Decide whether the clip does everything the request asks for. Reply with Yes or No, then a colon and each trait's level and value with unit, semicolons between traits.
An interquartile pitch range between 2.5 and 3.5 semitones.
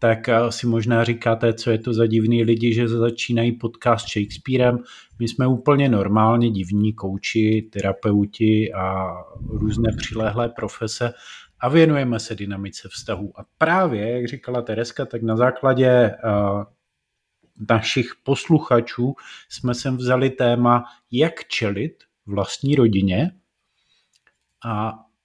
No: narrow, 2.1 semitones